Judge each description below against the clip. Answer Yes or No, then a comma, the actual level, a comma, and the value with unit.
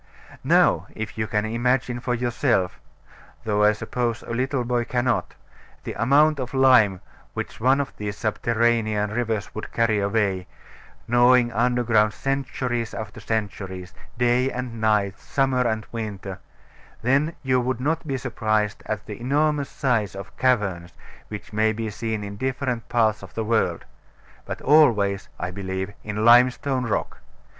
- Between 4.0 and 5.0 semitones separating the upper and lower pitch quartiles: No, average, 3.1 semitones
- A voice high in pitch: No, low, 115 Hz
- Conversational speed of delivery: Yes, average, 145 wpm